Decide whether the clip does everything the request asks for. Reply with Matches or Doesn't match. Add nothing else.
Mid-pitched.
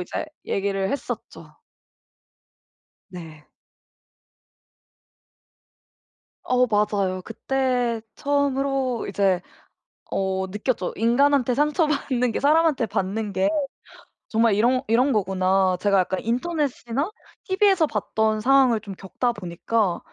Doesn't match